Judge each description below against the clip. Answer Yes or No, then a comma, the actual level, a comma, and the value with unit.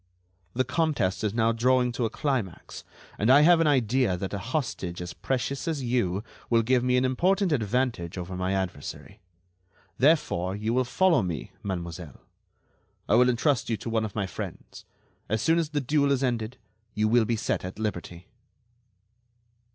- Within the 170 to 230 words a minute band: Yes, average, 175 wpm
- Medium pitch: No, low, 120 Hz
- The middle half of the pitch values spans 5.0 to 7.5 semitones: Yes, wide, 5.5 semitones